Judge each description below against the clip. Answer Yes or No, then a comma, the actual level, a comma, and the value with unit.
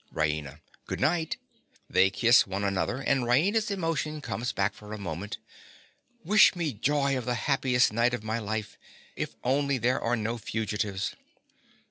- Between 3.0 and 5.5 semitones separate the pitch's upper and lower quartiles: Yes, average, 5.1 semitones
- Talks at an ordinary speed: Yes, average, 150 wpm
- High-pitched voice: No, low, 120 Hz